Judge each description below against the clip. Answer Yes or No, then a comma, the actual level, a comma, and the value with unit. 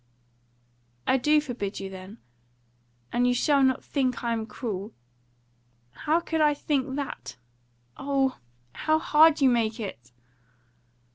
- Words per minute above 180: No, slow, 135 wpm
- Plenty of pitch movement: Yes, wide, 6.5 semitones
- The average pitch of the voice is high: Yes, very high, 250 Hz